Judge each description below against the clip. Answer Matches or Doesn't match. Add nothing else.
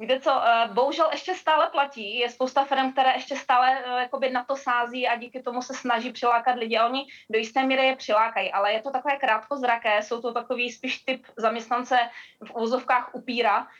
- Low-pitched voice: Doesn't match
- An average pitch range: Doesn't match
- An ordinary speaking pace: Doesn't match